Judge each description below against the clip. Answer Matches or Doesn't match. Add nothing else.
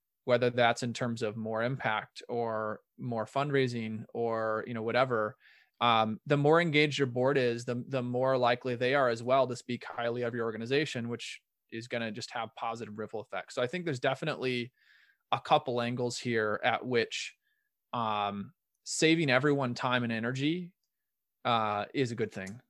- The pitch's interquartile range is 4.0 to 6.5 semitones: Doesn't match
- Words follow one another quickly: Doesn't match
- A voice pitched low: Matches